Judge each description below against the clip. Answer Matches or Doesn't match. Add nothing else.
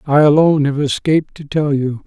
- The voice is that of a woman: Doesn't match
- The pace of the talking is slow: Doesn't match